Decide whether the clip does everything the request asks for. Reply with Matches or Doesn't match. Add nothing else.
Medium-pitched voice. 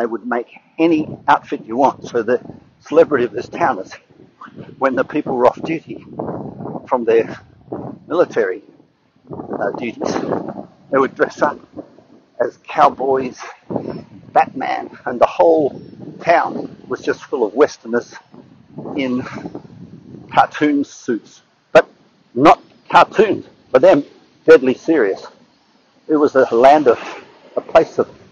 Matches